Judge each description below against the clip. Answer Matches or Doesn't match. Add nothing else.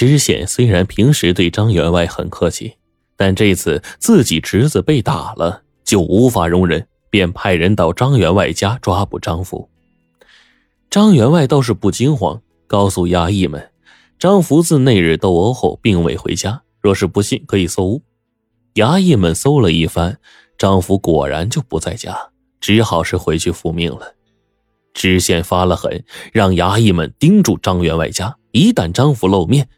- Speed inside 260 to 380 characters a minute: Doesn't match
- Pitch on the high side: Doesn't match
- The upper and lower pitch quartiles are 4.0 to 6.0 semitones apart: Matches